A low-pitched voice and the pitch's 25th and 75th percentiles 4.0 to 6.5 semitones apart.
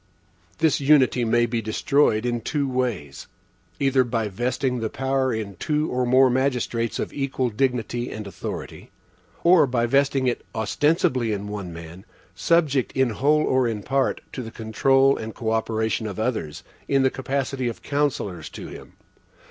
No: low, 125 Hz; average, 3.5 semitones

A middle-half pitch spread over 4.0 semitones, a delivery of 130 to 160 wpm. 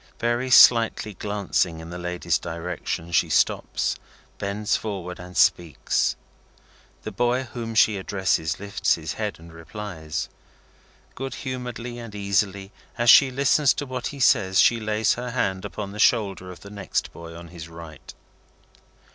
Yes: average, 5.1 semitones; average, 150 wpm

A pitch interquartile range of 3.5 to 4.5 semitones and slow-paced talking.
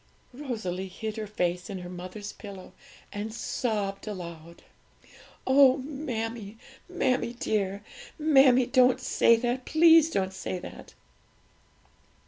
No: average, 5.2 semitones; slow, 110 wpm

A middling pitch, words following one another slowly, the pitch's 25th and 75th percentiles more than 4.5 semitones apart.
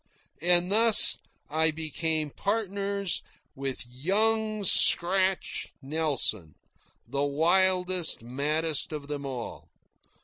Yes: medium, 160 Hz; slow, 90 wpm; average, 5.2 semitones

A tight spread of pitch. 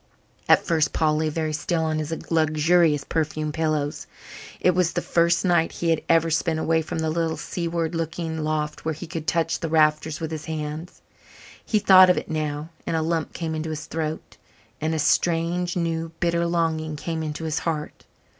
Yes: narrow, 1.3 semitones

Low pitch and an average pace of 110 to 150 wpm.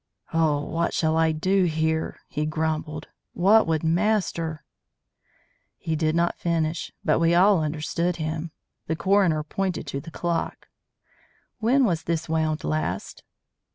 No: medium, 160 Hz; average, 140 wpm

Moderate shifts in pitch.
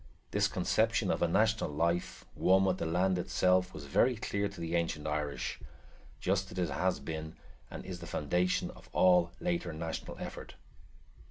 No: narrow, 2.2 semitones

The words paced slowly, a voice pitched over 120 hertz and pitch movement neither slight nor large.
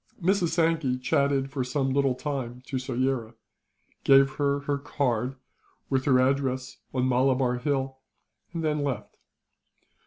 No: slow, 130 wpm; low, 135 Hz; narrow, 1.8 semitones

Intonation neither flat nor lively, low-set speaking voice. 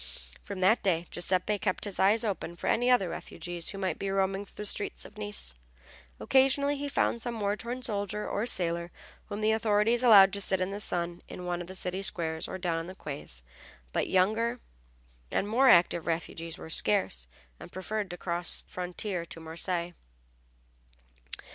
No: average, 3.5 semitones; high, 190 Hz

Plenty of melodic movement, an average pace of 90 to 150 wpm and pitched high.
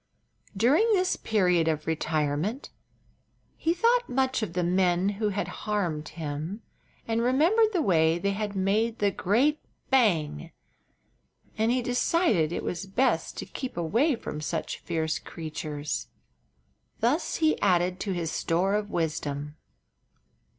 Yes: wide, 7.1 semitones; slow, 135 wpm; high, 195 Hz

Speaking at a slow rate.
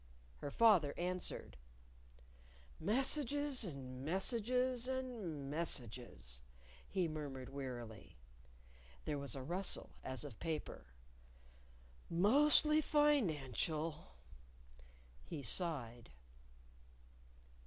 Yes: slow, 75 wpm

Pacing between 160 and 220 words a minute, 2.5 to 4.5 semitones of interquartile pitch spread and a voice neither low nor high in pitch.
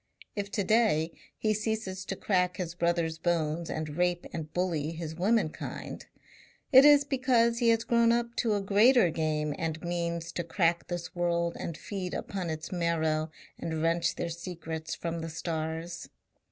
Yes: average, 165 wpm; average, 3.9 semitones; medium, 170 Hz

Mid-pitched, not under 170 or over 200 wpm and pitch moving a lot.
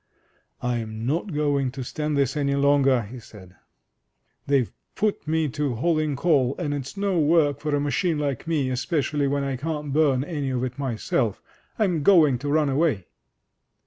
No: medium, 145 Hz; average, 175 wpm; average, 3.0 semitones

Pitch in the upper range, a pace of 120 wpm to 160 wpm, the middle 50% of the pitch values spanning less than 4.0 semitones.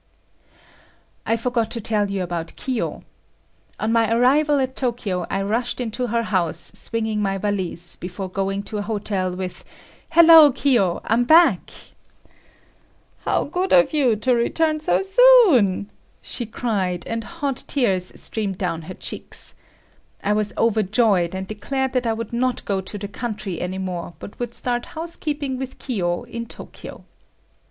No: high, 225 Hz; average, 150 wpm; average, 4.8 semitones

